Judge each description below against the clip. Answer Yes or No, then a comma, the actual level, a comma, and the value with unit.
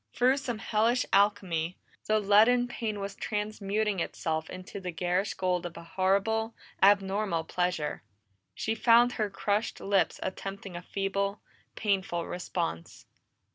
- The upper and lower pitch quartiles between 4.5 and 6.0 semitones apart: No, average, 3.0 semitones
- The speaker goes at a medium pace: No, slow, 130 wpm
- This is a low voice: No, high, 200 Hz